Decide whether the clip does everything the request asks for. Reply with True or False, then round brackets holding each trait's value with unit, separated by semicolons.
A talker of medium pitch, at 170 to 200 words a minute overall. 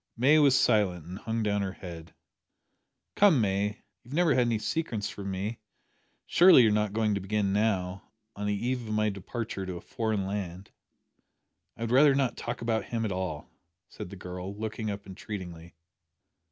False (105 Hz; 180 wpm)